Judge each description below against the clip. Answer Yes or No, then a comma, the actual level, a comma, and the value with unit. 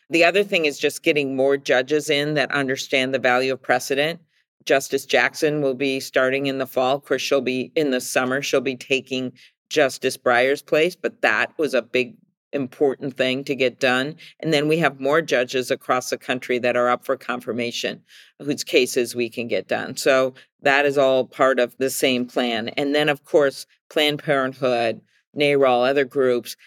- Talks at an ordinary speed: Yes, average, 190 wpm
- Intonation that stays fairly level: Yes, narrow, 2.2 semitones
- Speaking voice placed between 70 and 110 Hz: No, low, 135 Hz